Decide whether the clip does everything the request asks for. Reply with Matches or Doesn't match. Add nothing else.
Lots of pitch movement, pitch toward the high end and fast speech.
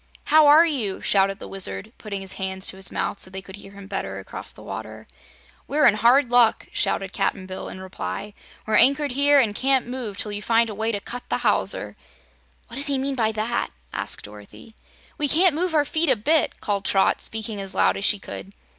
Matches